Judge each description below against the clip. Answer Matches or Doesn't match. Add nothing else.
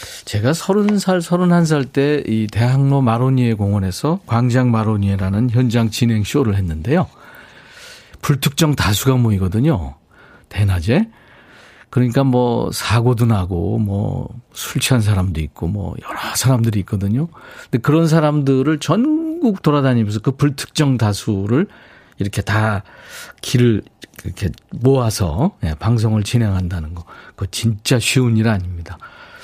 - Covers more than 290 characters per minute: Doesn't match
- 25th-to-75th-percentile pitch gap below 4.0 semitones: Doesn't match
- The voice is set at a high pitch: Doesn't match